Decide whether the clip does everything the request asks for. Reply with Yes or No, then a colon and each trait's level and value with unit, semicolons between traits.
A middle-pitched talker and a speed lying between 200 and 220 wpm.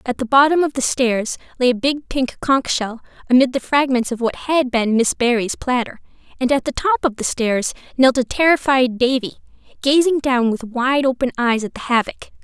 No: very high, 255 Hz; fast, 205 wpm